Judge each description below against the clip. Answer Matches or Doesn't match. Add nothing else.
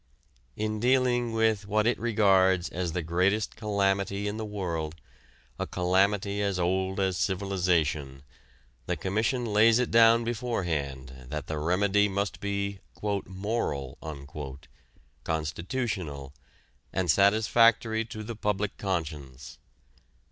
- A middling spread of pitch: Matches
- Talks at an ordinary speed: Doesn't match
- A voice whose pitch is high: Doesn't match